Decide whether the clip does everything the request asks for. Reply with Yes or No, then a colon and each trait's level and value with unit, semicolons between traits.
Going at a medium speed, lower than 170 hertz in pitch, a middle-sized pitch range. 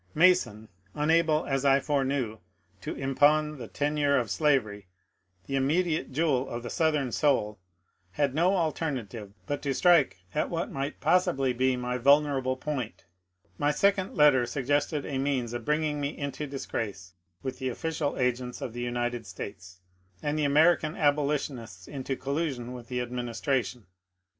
Yes: average, 150 wpm; low, 135 Hz; average, 3.6 semitones